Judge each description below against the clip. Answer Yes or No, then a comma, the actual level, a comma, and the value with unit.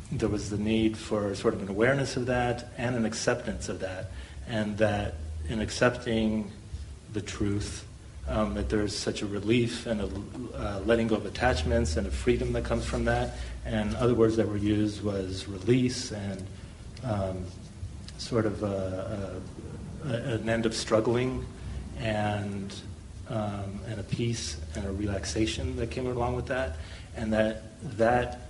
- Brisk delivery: No, average, 160 wpm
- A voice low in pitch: Yes, low, 105 Hz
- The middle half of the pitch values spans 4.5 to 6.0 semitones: No, average, 2.9 semitones